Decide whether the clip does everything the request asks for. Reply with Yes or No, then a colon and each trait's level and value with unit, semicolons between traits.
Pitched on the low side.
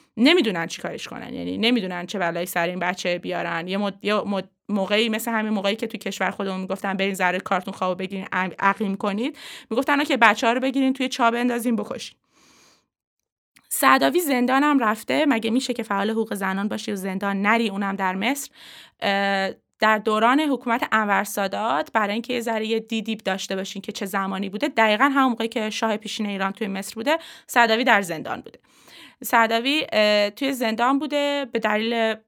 No: high, 220 Hz